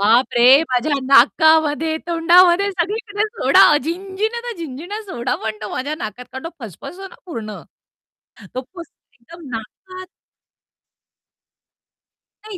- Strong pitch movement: Yes, wide, 6.8 semitones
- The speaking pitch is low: No, very high, 330 Hz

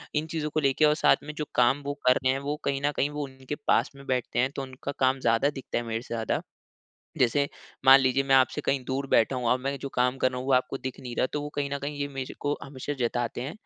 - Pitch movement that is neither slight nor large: No, narrow, 2.0 semitones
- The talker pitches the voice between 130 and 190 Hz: Yes, low, 135 Hz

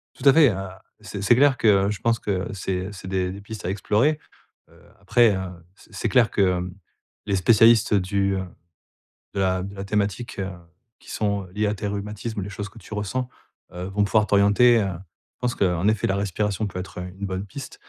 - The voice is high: No, low, 100 Hz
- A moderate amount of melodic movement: No, narrow, 2.3 semitones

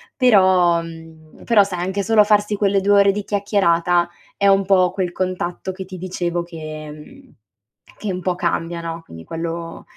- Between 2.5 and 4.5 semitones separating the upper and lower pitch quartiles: Yes, average, 2.9 semitones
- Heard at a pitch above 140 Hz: Yes, medium, 185 Hz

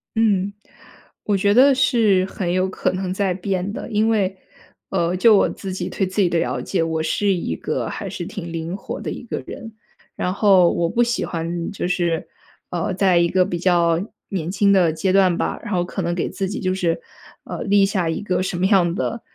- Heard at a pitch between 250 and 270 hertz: No, medium, 185 Hz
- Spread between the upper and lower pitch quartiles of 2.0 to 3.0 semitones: Yes, narrow, 2.6 semitones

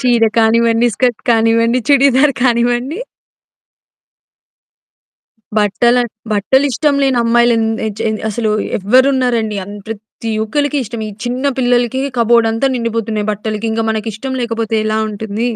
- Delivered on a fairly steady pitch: Yes, narrow, 2.2 semitones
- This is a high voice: Yes, high, 235 Hz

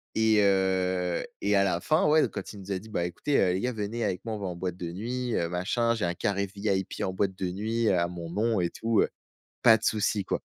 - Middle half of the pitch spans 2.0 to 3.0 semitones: No, average, 3.5 semitones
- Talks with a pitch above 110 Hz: No, low, 100 Hz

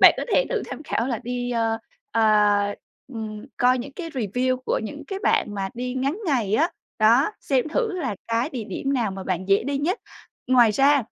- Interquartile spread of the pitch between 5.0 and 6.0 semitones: No, average, 4.4 semitones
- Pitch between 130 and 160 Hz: No, high, 245 Hz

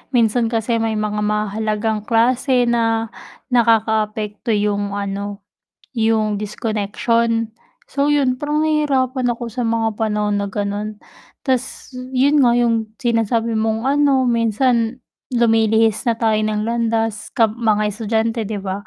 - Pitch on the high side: Yes, high, 225 Hz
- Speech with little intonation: Yes, narrow, 2.1 semitones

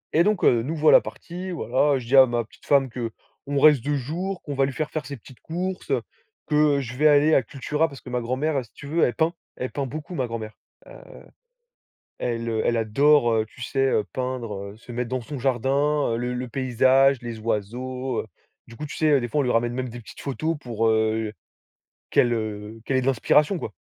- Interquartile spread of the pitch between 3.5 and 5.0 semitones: Yes, average, 3.9 semitones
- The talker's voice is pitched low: Yes, low, 130 Hz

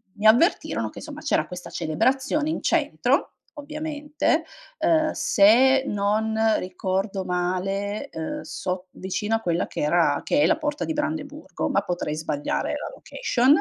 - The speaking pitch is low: No, high, 215 Hz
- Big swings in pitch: Yes, wide, 8.3 semitones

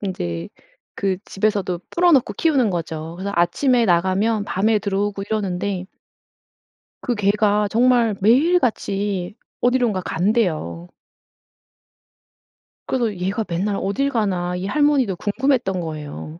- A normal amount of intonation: Yes, average, 4.4 semitones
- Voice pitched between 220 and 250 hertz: No, high, 200 Hz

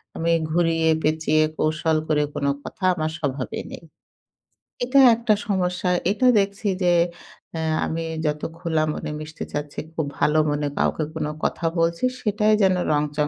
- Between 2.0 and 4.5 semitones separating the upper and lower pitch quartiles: Yes, average, 2.9 semitones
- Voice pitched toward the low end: No, medium, 160 Hz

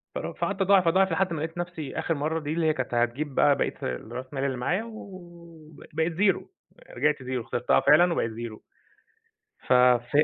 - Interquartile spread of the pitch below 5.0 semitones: No, wide, 5.4 semitones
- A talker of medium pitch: Yes, medium, 155 Hz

